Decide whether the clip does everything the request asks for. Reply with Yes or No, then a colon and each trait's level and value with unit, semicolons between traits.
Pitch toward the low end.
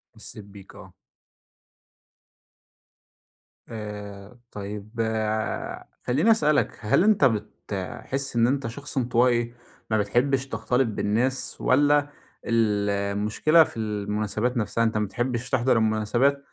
Yes: low, 115 Hz